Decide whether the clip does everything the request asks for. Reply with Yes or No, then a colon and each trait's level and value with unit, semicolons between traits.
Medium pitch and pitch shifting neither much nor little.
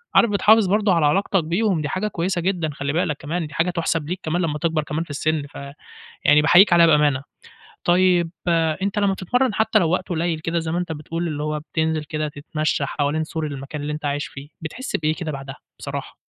Yes: medium, 160 Hz; average, 3.2 semitones